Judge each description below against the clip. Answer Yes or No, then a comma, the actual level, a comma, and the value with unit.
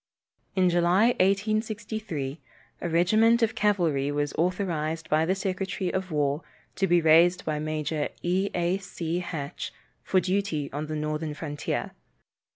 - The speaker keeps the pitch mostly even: No, average, 3.8 semitones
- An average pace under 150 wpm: Yes, average, 140 wpm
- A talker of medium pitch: Yes, medium, 175 Hz